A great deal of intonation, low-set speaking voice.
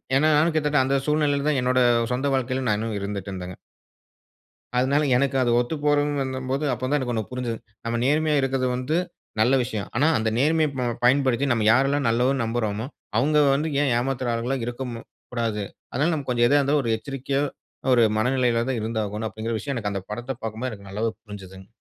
No: average, 3.6 semitones; low, 125 Hz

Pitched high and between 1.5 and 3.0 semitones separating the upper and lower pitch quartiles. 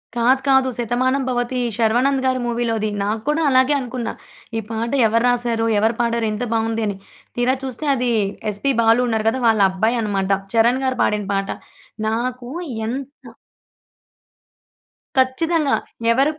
Yes: high, 240 Hz; narrow, 2.5 semitones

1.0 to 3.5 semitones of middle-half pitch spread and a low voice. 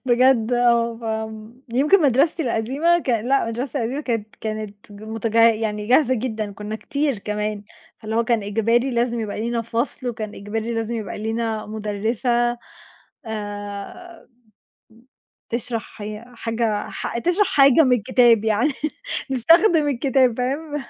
No: average, 2.9 semitones; high, 230 Hz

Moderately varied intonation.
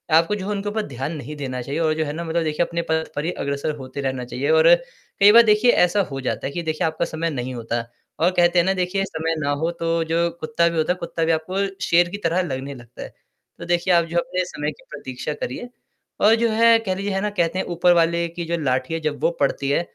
Yes: average, 3.5 semitones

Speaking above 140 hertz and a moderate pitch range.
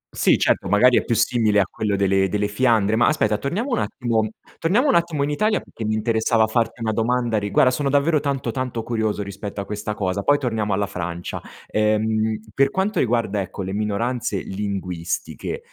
No: low, 110 Hz; average, 3.7 semitones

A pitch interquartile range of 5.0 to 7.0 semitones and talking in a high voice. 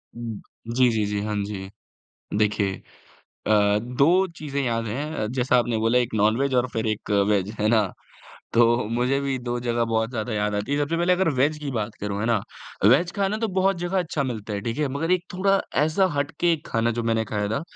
No: average, 5.3 semitones; low, 120 Hz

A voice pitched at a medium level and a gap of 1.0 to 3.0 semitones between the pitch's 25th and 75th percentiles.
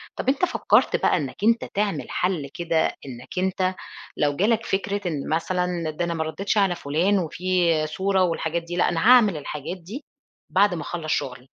No: medium, 175 Hz; average, 3.6 semitones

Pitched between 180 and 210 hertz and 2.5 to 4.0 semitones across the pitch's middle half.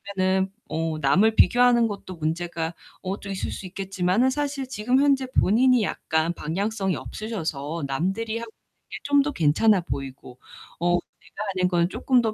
No: high, 190 Hz; wide, 5.4 semitones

